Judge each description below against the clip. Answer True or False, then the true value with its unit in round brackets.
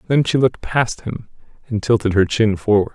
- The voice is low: True (115 Hz)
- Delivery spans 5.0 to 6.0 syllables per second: True (5.5 syllables/s)